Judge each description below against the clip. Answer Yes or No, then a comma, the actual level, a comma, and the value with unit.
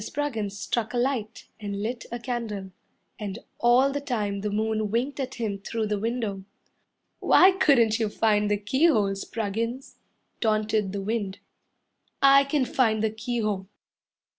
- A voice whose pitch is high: Yes, high, 220 Hz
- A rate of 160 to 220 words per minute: No, average, 145 wpm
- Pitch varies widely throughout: No, average, 3.2 semitones